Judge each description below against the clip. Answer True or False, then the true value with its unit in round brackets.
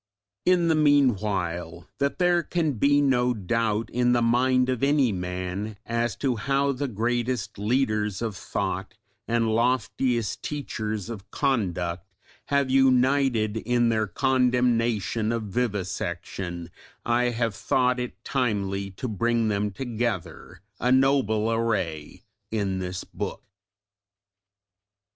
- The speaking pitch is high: False (115 Hz)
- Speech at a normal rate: False (120 wpm)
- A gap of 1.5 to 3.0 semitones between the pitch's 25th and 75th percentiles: False (4.0 semitones)